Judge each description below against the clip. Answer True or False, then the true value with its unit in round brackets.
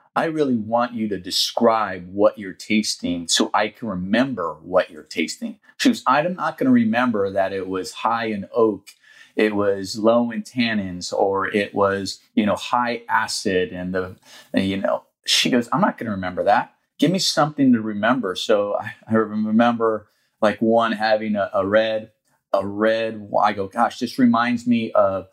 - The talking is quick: False (180 wpm)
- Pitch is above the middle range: False (110 Hz)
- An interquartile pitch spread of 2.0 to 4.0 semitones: True (3.3 semitones)